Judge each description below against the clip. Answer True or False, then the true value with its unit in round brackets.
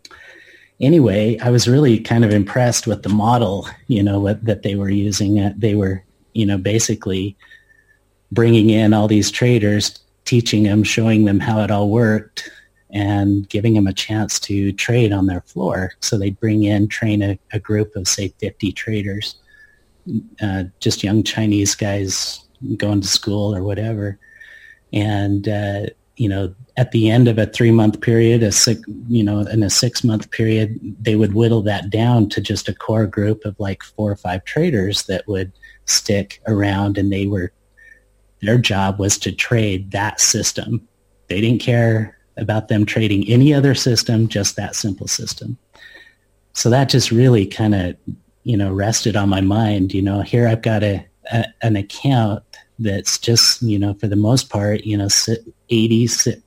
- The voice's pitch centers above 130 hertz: False (105 Hz)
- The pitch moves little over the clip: True (2.3 semitones)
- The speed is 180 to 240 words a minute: False (170 wpm)